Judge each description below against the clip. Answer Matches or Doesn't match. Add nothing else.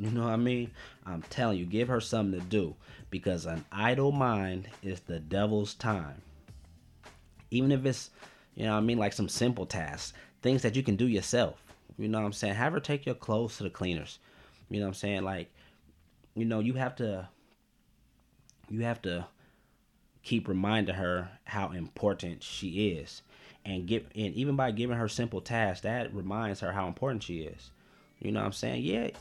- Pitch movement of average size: Matches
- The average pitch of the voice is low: Matches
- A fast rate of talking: Doesn't match